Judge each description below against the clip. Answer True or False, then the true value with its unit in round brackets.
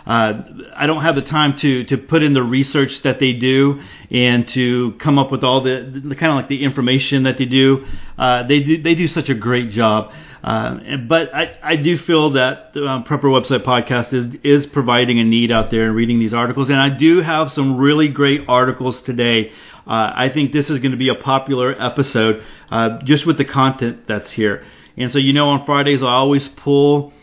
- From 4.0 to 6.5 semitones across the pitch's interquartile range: False (2.6 semitones)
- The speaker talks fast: True (225 wpm)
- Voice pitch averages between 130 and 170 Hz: True (135 Hz)